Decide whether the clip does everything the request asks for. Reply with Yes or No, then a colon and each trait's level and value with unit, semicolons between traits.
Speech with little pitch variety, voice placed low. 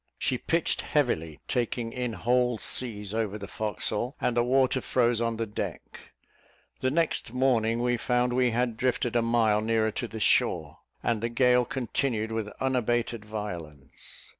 Yes: narrow, 2.3 semitones; low, 120 Hz